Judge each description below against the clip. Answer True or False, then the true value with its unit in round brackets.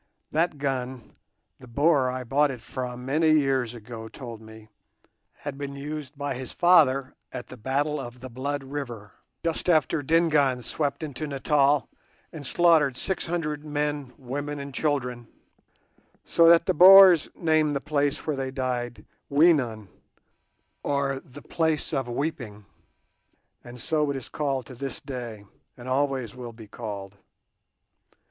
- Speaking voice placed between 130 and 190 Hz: True (140 Hz)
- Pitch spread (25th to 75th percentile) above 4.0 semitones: False (3.2 semitones)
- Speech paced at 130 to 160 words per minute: True (145 wpm)